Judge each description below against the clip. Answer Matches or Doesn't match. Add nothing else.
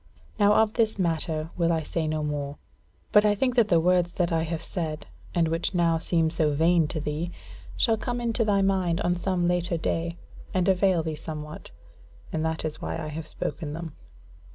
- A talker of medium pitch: Matches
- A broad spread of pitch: Doesn't match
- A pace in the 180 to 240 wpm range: Matches